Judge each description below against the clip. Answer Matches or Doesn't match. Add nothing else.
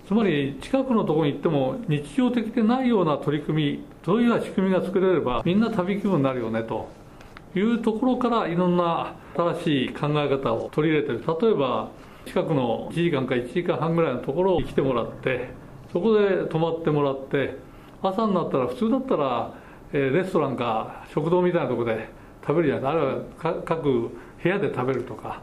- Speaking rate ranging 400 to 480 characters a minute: Doesn't match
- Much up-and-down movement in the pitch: Matches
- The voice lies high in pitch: Doesn't match